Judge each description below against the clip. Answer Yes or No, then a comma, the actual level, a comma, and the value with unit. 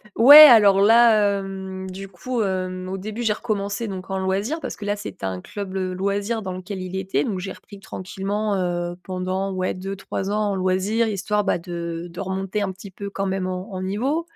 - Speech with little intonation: Yes, narrow, 1.9 semitones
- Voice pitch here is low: No, high, 195 Hz